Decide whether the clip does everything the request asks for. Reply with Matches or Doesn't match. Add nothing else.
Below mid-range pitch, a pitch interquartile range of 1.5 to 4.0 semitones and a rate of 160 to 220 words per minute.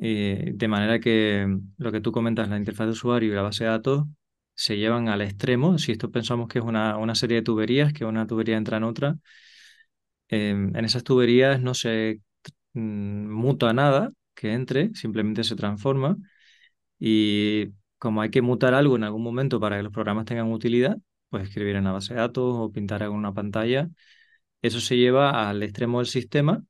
Matches